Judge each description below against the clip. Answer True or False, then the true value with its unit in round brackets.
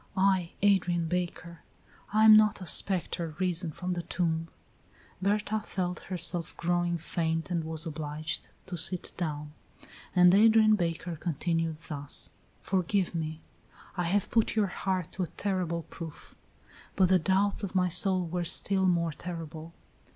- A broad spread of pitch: False (2.4 semitones)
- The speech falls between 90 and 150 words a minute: True (145 wpm)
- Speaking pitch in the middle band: True (175 Hz)